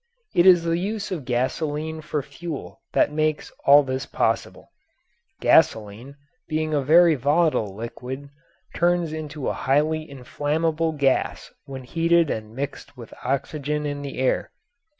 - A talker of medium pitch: Yes, medium, 150 Hz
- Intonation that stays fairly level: No, average, 3.2 semitones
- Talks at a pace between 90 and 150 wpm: Yes, average, 140 wpm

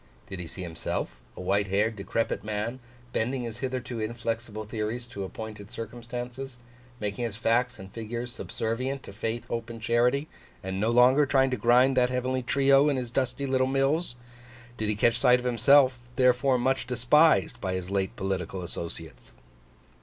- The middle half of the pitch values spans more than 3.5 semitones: No, average, 3.2 semitones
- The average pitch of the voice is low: Yes, low, 120 Hz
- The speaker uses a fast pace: No, average, 170 wpm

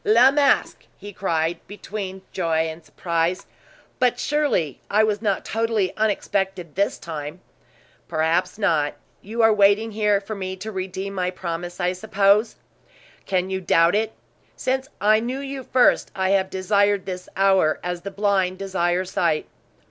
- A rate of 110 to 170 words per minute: Yes, average, 150 wpm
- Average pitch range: Yes, average, 3.2 semitones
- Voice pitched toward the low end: No, high, 195 Hz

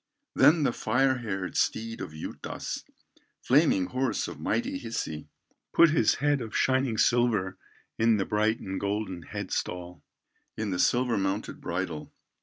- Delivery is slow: No, average, 145 wpm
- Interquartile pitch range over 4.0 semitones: Yes, average, 4.8 semitones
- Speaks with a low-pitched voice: Yes, low, 110 Hz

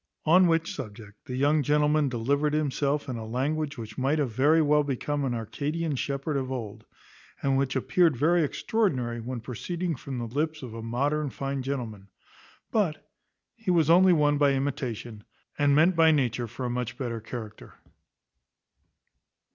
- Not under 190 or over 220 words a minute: No, average, 165 wpm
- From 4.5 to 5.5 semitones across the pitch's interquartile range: No, average, 3.9 semitones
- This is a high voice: No, medium, 140 Hz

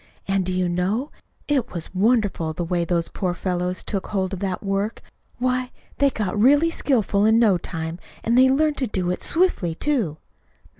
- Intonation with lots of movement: Yes, wide, 5.8 semitones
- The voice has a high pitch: Yes, high, 200 Hz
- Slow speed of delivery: No, average, 185 wpm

